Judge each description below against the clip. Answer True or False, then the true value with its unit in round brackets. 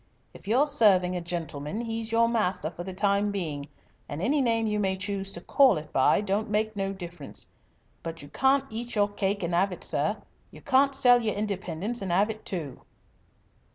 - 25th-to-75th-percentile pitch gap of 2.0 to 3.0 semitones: False (4.2 semitones)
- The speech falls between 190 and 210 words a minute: True (195 wpm)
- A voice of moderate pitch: False (200 Hz)